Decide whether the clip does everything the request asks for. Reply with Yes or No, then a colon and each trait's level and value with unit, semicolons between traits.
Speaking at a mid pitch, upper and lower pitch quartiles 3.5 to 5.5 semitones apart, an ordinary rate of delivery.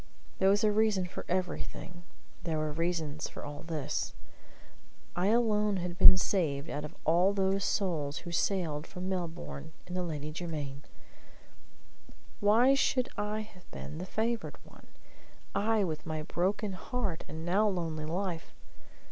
Yes: medium, 180 Hz; average, 4.3 semitones; average, 150 wpm